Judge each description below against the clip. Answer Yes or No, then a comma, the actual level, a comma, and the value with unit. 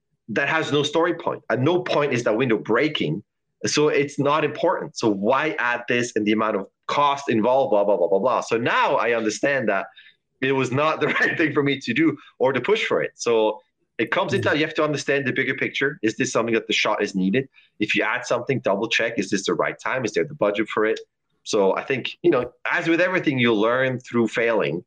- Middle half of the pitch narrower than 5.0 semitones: No, average, 5.3 semitones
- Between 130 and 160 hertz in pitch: Yes, medium, 140 Hz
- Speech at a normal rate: No, fast, 240 wpm